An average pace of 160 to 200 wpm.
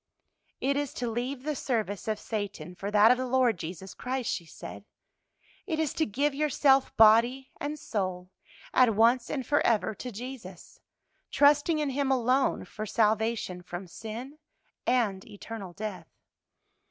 No: average, 150 wpm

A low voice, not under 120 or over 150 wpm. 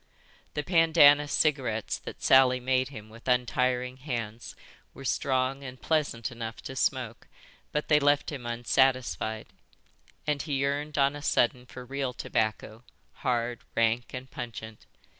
Yes: low, 130 Hz; average, 140 wpm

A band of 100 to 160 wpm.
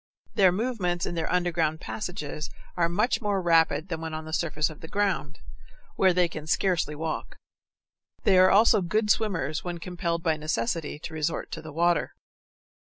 No: average, 170 wpm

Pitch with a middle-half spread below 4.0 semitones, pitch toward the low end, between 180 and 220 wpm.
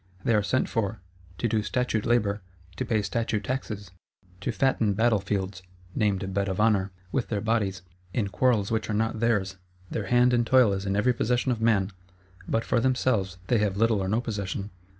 Yes: average, 2.8 semitones; low, 105 Hz; average, 190 wpm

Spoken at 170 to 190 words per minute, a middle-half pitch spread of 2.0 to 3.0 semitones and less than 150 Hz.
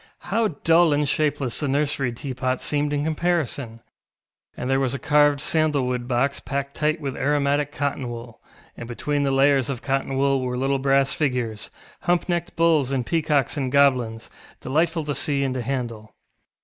Yes: average, 175 wpm; narrow, 2.5 semitones; medium, 140 Hz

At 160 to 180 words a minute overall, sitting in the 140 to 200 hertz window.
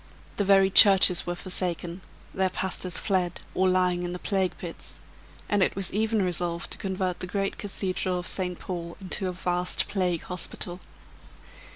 Yes: average, 165 wpm; medium, 185 Hz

